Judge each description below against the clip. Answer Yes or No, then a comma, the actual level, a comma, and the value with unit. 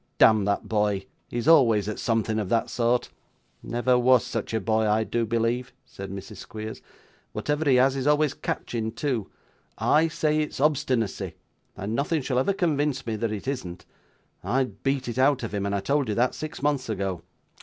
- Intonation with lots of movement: No, average, 4.2 semitones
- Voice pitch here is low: Yes, low, 120 Hz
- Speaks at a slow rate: No, average, 185 wpm